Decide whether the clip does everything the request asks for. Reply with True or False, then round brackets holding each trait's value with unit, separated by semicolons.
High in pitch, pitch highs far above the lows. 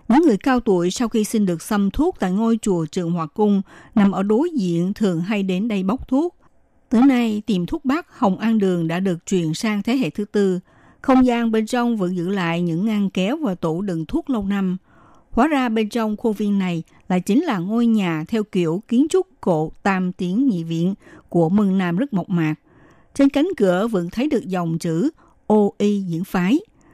False (200 Hz; 4.6 semitones)